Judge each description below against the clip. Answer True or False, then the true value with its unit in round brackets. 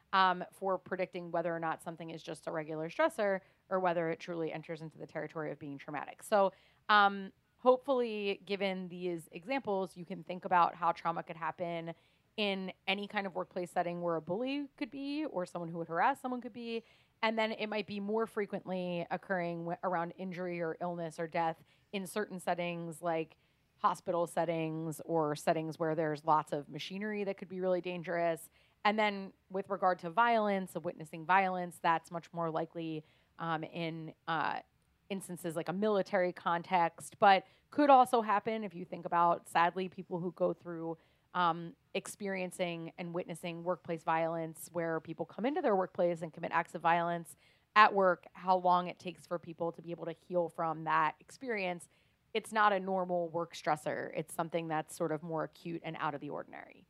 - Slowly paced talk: False (185 wpm)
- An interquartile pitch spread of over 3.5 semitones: False (2.6 semitones)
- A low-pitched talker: False (175 Hz)